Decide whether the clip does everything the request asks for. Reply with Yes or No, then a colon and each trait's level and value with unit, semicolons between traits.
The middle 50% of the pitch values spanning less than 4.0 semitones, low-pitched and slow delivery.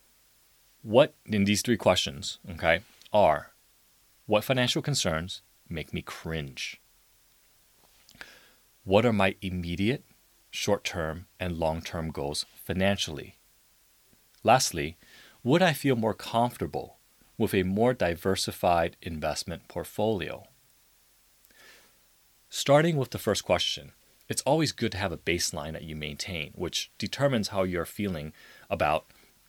No: average, 5.3 semitones; low, 100 Hz; slow, 115 wpm